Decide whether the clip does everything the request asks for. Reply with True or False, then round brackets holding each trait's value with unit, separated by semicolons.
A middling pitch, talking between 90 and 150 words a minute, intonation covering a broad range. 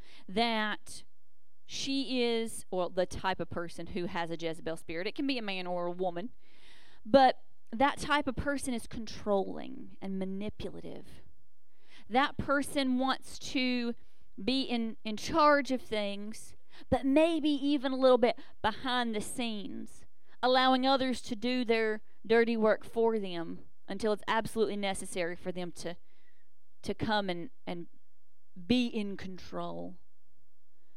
False (220 Hz; 140 wpm; 5.7 semitones)